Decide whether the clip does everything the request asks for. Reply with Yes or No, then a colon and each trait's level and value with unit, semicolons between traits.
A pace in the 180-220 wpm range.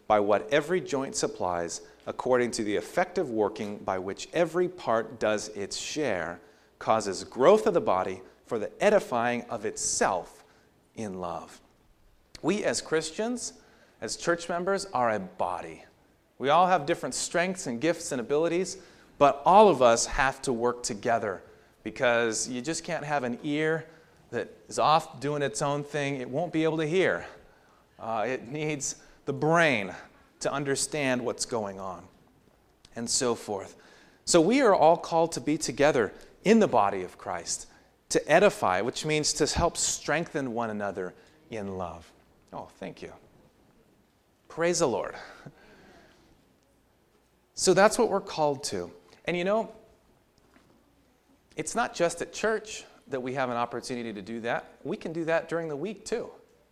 No: average, 155 wpm